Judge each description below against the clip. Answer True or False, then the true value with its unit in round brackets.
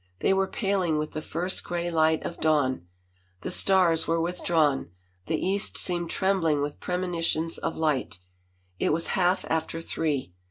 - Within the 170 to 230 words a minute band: False (155 wpm)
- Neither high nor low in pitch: True (165 Hz)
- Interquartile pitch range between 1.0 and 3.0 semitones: True (2.5 semitones)